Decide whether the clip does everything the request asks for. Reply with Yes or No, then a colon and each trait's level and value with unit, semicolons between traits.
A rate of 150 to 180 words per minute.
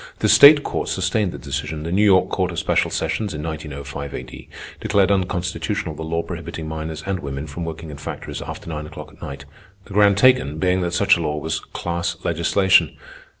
No: average, 195 wpm